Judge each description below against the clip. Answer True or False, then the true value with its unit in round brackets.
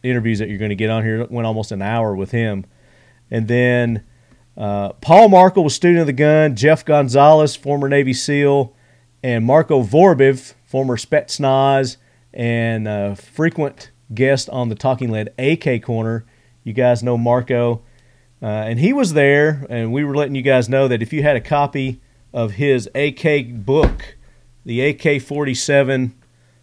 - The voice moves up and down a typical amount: True (3.4 semitones)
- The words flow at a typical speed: True (160 wpm)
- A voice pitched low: True (125 Hz)